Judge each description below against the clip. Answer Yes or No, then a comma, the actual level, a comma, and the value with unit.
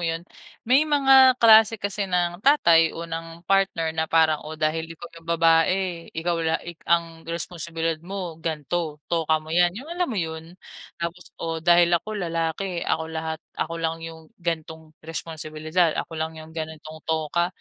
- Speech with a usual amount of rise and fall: No, narrow, 1.7 semitones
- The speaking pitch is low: No, medium, 165 Hz